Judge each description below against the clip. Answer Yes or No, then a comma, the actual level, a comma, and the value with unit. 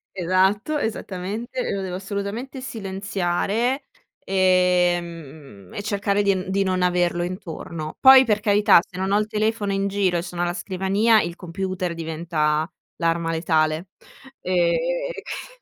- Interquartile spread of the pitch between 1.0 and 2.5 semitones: No, average, 2.9 semitones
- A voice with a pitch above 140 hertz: Yes, medium, 185 Hz